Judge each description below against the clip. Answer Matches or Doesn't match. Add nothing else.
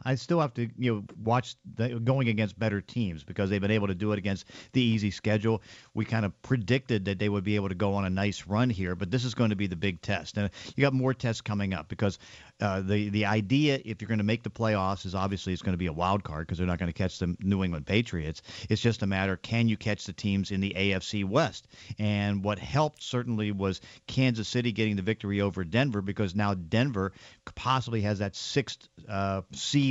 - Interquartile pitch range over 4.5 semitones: Doesn't match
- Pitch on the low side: Matches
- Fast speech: Matches